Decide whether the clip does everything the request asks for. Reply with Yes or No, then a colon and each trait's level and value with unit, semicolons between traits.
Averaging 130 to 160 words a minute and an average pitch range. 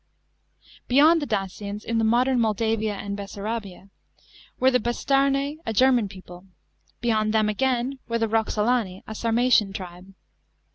Yes: slow, 135 wpm; average, 3.7 semitones